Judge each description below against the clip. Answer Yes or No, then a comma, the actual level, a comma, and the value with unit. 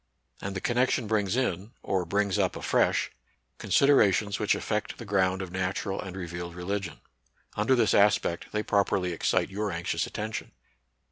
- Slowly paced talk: No, average, 155 wpm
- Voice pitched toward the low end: Yes, low, 100 Hz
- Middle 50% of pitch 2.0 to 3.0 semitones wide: Yes, narrow, 2.4 semitones